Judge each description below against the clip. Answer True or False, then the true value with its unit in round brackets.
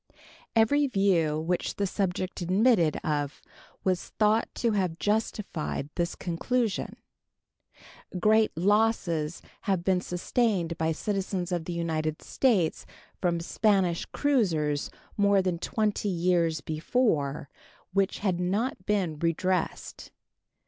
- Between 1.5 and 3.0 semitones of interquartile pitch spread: False (3.9 semitones)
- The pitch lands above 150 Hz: True (185 Hz)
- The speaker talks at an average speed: False (110 wpm)